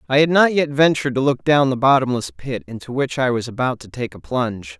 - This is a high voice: No, low, 125 Hz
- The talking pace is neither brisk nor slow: No, fast, 250 wpm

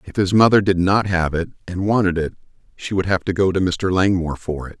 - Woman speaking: No, male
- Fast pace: Yes, fast, 250 wpm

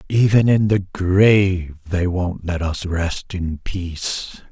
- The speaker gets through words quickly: No, average, 145 wpm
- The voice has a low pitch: Yes, very low, 90 Hz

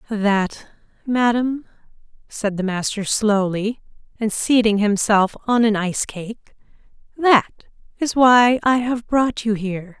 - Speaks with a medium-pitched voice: No, high, 220 Hz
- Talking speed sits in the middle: No, slow, 120 wpm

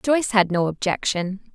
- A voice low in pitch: No, high, 205 Hz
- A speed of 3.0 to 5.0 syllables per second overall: Yes, 4.6 syllables/s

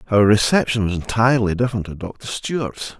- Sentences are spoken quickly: No, average, 160 wpm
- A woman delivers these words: No, male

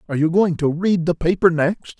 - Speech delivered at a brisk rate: Yes, fast, 240 wpm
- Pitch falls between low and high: Yes, medium, 170 Hz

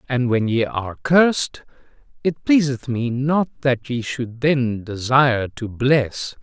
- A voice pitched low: Yes, low, 130 Hz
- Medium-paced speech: Yes, average, 150 wpm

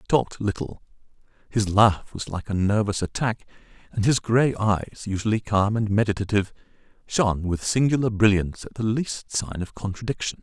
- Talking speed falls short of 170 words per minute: Yes, average, 160 wpm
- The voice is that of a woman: No, male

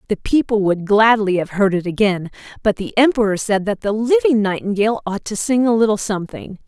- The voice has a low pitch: No, high, 210 Hz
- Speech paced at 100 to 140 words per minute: No, average, 200 wpm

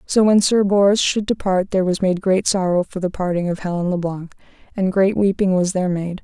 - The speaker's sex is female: Yes, female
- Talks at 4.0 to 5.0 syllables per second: No, 5.6 syllables/s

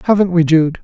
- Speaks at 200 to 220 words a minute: Yes, fast, 215 wpm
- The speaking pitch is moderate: Yes, medium, 170 Hz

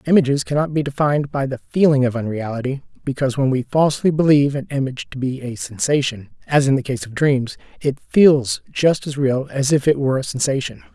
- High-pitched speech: No, low, 135 Hz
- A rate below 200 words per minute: No, fast, 205 wpm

